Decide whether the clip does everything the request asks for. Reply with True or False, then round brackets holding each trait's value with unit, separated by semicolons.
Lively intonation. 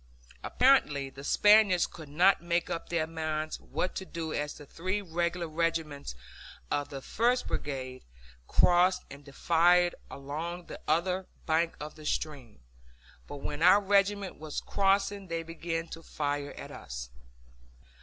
False (3.6 semitones)